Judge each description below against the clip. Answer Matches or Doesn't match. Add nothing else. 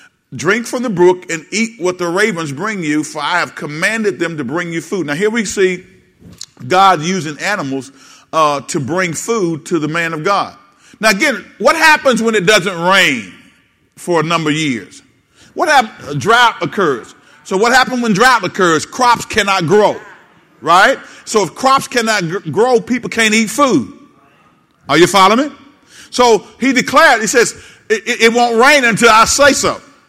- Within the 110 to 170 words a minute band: Doesn't match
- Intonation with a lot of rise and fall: Matches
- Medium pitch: Doesn't match